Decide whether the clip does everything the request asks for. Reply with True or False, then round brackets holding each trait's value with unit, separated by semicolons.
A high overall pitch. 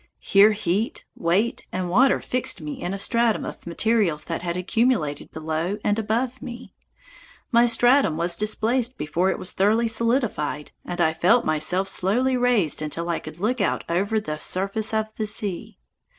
True (200 Hz)